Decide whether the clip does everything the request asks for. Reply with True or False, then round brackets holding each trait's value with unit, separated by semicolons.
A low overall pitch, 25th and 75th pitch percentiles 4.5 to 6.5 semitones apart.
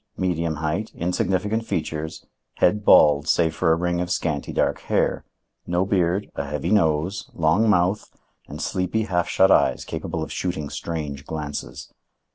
False (85 Hz; 3.2 semitones)